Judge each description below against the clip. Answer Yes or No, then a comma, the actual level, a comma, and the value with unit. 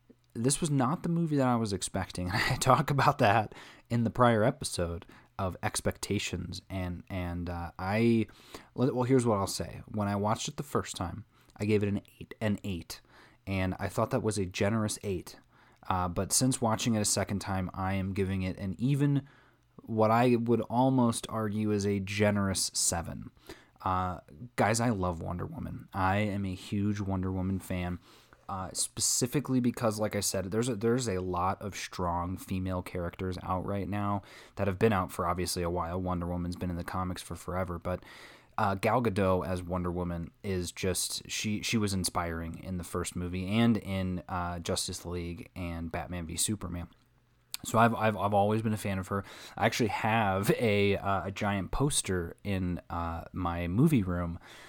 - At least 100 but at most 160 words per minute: No, average, 185 wpm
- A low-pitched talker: Yes, low, 100 Hz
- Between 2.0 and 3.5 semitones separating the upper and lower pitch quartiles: No, average, 3.9 semitones